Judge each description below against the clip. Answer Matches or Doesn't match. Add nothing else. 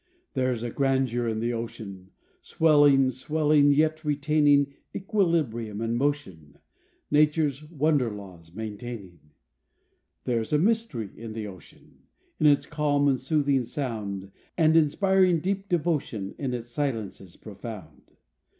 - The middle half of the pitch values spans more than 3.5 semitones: Matches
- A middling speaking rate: Doesn't match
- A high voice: Doesn't match